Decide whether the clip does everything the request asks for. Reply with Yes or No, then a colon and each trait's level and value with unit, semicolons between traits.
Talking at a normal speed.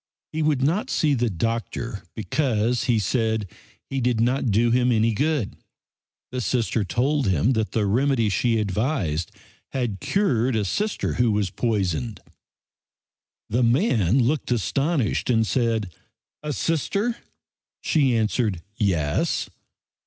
No: slow, 130 wpm